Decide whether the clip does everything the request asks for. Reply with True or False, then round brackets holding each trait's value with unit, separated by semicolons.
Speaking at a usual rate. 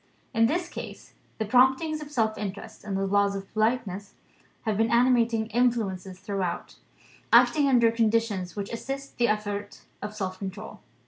True (150 wpm)